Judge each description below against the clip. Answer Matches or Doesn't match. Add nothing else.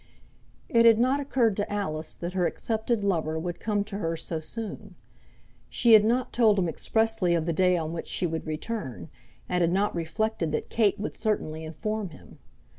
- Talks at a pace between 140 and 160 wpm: Doesn't match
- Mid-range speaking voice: Doesn't match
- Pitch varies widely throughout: Doesn't match